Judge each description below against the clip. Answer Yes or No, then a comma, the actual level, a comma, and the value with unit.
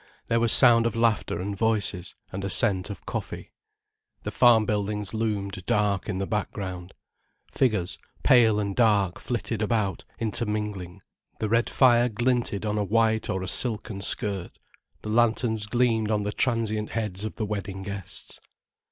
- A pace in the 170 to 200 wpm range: No, average, 155 wpm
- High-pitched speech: No, low, 105 Hz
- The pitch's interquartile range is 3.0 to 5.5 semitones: No, narrow, 2.5 semitones